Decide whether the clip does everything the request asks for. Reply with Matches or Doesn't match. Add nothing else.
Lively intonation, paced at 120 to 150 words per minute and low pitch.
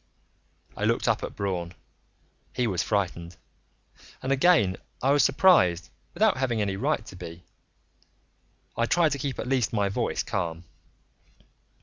Matches